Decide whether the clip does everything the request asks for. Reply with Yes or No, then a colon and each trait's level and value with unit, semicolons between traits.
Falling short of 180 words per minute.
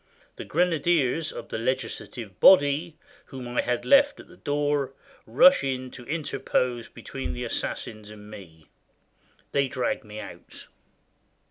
Yes: slow, 135 wpm